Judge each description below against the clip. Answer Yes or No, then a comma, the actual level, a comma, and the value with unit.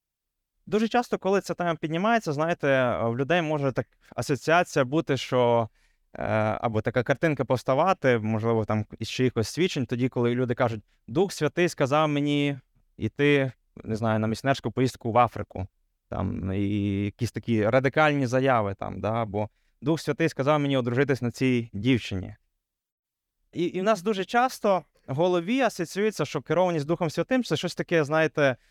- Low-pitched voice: Yes, low, 130 Hz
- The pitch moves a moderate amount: No, wide, 6.5 semitones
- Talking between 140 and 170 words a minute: Yes, fast, 155 wpm